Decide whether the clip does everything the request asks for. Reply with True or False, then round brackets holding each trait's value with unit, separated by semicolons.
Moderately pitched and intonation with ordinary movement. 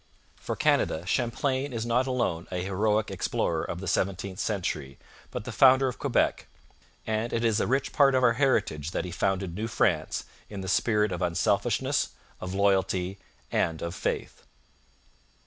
False (100 Hz; 4.7 semitones)